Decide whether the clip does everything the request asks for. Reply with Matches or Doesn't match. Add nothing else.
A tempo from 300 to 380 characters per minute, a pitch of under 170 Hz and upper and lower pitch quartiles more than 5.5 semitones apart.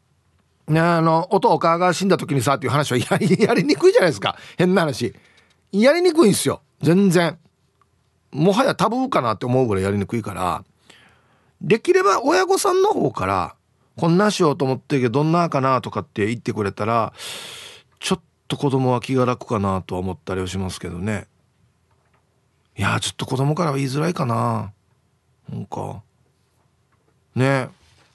Matches